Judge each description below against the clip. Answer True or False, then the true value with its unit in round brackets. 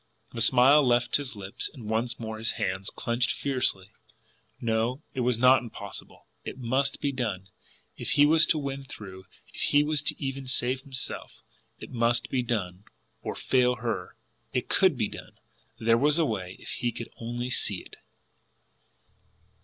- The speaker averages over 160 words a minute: True (170 wpm)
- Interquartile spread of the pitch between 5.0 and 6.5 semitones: False (3.2 semitones)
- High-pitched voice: False (120 Hz)